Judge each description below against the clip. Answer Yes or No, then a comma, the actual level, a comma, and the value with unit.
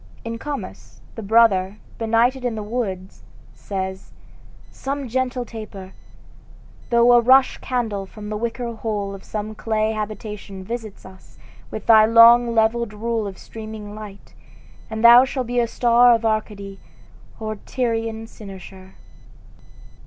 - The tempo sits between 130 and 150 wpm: Yes, average, 140 wpm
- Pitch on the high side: Yes, high, 220 Hz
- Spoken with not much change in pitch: Yes, narrow, 2.2 semitones